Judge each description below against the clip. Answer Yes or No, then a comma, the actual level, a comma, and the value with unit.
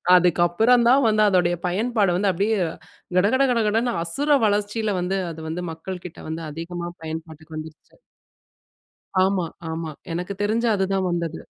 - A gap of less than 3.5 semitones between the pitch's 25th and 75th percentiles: No, average, 4.2 semitones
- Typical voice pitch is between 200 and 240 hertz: No, medium, 185 Hz